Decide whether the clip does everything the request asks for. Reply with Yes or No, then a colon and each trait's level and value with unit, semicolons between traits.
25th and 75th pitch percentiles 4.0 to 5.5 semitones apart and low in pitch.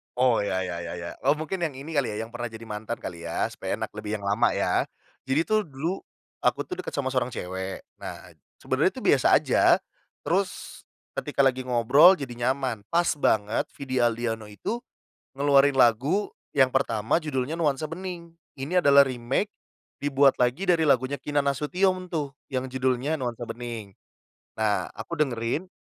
Yes: average, 4.8 semitones; low, 130 Hz